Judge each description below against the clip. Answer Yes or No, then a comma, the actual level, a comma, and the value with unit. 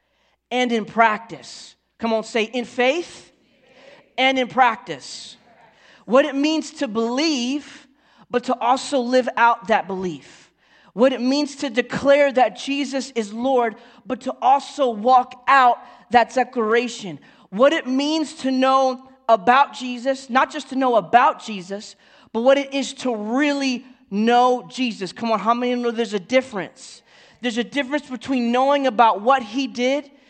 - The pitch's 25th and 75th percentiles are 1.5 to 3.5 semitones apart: Yes, average, 2.7 semitones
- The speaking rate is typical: Yes, average, 155 wpm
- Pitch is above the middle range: Yes, very high, 255 Hz